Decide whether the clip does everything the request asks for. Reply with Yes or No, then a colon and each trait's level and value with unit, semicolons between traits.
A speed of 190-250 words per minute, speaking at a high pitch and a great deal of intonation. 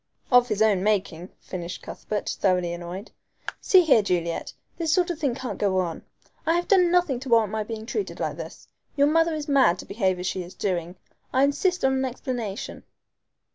Yes: average, 195 wpm; high, 225 Hz; wide, 7.7 semitones